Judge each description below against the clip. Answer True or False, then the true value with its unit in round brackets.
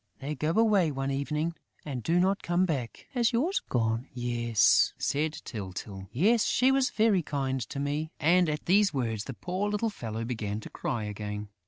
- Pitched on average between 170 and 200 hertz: False (145 Hz)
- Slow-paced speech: False (175 wpm)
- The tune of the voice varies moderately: False (7.7 semitones)